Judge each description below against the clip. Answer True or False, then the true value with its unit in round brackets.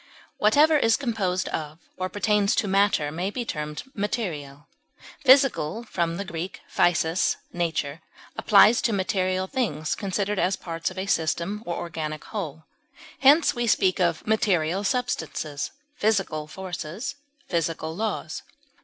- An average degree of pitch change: True (4.9 semitones)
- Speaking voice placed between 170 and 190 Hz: True (185 Hz)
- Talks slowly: True (125 wpm)